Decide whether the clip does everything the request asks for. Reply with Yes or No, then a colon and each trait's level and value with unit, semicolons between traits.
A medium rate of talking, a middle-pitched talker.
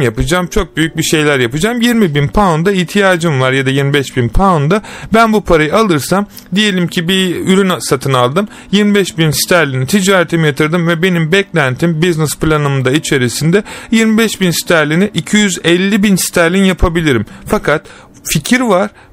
No: fast, 145 wpm; medium, 175 Hz